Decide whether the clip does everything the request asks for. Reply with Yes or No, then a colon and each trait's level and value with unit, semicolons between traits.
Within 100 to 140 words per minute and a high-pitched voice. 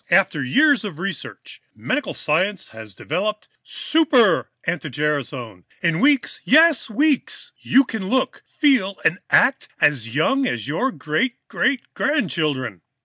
Yes: slow, 135 wpm; high, 195 Hz